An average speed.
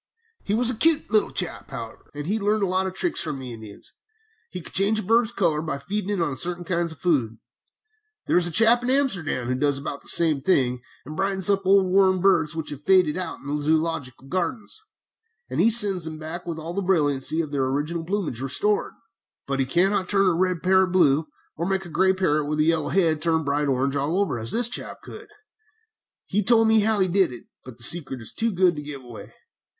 No: fast, 230 wpm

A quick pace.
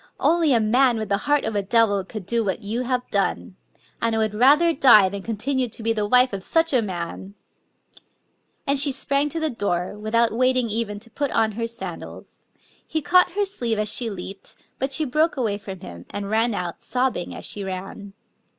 Yes: fast, 210 wpm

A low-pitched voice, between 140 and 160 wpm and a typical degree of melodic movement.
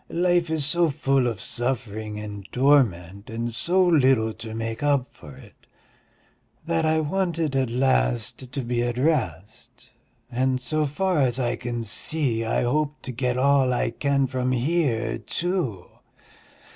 Yes: low, 130 Hz; average, 150 wpm; average, 4.8 semitones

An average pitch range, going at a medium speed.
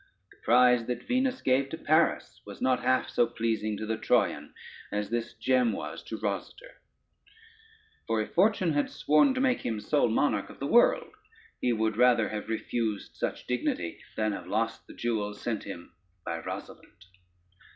Yes: average, 5.0 semitones; average, 170 wpm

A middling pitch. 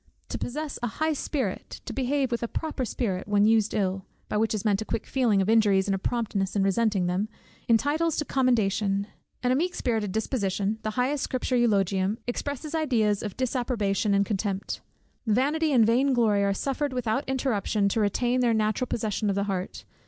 No: high, 220 Hz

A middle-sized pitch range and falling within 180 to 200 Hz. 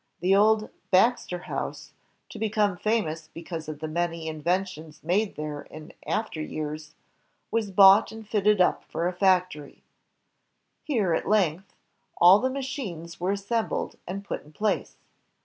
Yes: average, 4.7 semitones; medium, 185 Hz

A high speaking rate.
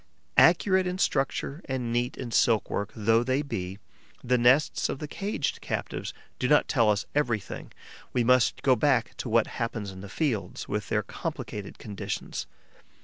No: average, 165 wpm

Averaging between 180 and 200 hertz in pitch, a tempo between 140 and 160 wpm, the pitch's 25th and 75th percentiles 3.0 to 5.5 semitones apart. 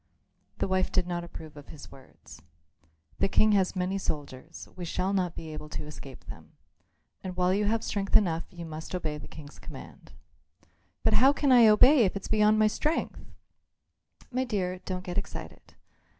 No: medium, 185 Hz; average, 180 wpm; average, 4.5 semitones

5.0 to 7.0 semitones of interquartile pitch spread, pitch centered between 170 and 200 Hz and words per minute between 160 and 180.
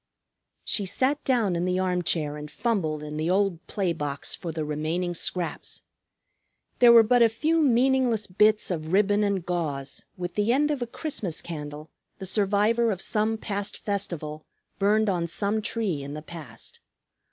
Yes: average, 5.3 semitones; high, 190 Hz; average, 165 wpm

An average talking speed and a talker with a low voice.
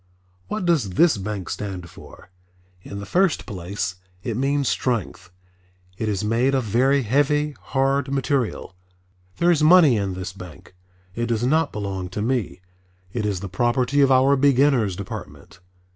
Yes: average, 155 wpm; low, 120 Hz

